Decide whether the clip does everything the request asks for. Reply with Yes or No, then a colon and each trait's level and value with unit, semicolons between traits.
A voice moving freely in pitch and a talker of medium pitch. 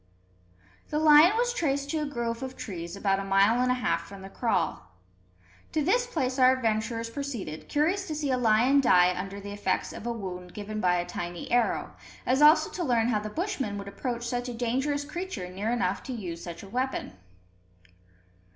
No: wide, 6.1 semitones; high, 235 Hz